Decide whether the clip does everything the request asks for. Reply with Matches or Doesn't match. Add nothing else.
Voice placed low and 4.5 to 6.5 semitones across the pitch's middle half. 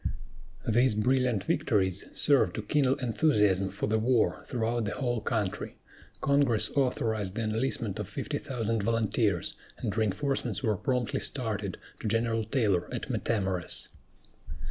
Doesn't match